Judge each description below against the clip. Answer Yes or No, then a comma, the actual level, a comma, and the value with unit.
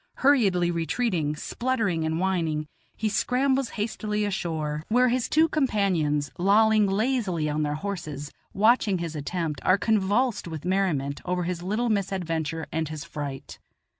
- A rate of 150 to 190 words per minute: No, slow, 135 wpm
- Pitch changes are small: No, wide, 5.4 semitones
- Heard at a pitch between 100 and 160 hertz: No, medium, 185 Hz